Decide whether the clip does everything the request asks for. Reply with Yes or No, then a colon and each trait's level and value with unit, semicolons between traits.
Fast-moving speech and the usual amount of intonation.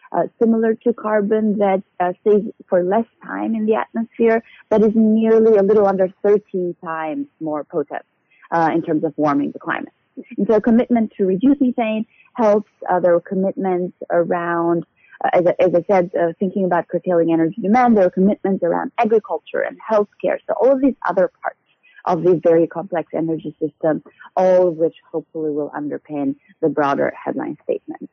No: average, 180 wpm; average, 4.8 semitones